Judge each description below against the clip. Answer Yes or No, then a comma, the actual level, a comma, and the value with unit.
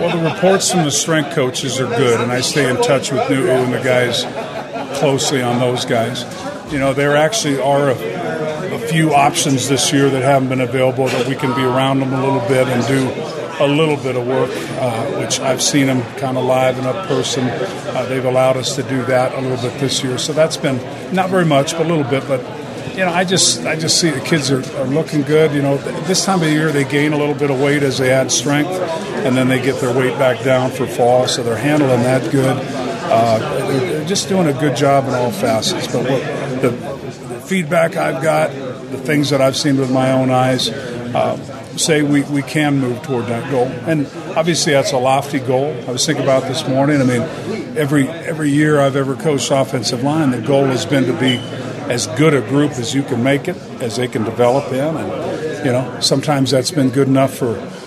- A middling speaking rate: No, fast, 225 wpm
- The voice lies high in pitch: No, low, 135 Hz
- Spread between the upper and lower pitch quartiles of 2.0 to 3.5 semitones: Yes, narrow, 2.4 semitones